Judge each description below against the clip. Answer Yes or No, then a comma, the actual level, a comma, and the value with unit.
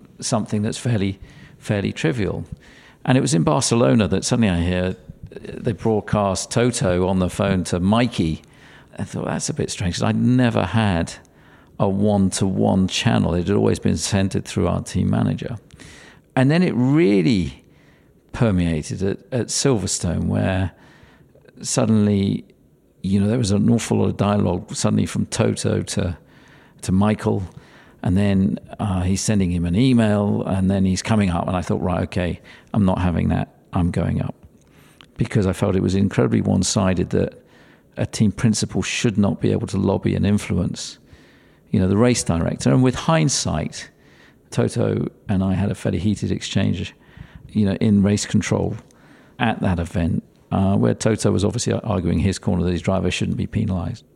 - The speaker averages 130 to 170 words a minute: Yes, average, 165 wpm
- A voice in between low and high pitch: No, low, 100 Hz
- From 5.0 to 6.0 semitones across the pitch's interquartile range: No, average, 3.4 semitones